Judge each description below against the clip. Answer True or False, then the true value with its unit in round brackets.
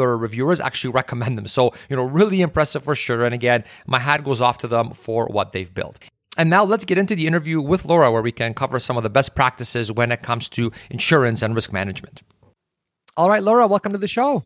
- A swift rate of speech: True (230 wpm)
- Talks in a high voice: False (130 Hz)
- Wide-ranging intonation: True (5.8 semitones)